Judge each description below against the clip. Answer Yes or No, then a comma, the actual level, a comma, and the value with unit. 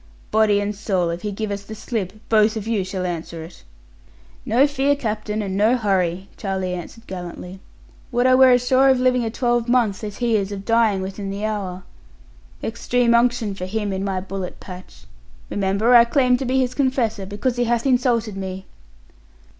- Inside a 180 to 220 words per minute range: Yes, average, 185 wpm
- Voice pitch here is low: No, high, 215 Hz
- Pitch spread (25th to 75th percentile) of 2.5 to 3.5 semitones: No, average, 3.9 semitones